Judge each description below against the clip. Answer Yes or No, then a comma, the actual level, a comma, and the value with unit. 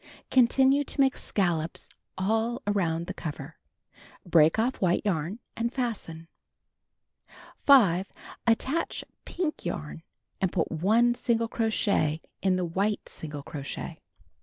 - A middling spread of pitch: No, wide, 6.2 semitones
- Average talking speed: No, slow, 115 wpm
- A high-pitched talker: Yes, high, 195 Hz